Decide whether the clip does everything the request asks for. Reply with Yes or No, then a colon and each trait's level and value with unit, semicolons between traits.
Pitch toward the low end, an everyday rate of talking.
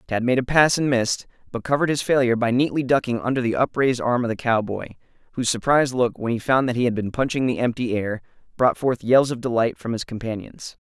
No: low, 120 Hz; fast, 230 wpm